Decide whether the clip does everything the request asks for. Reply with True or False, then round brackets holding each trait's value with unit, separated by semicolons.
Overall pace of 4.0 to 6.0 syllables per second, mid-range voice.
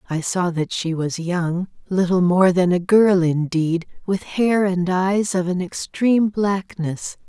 False (3.8 syllables/s; 180 Hz)